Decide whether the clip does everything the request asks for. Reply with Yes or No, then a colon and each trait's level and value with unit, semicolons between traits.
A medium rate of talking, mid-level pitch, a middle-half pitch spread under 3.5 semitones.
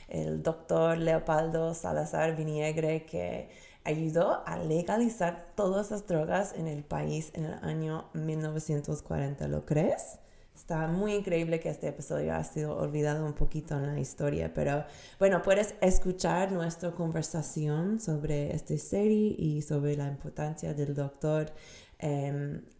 Yes: average, 135 wpm; medium, 155 Hz; narrow, 2.4 semitones